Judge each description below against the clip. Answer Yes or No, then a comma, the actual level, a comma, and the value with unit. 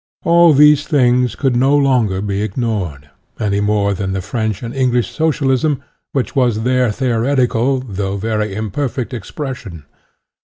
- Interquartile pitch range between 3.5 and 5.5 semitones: Yes, average, 4.6 semitones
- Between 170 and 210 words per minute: No, average, 145 wpm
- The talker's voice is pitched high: No, low, 120 Hz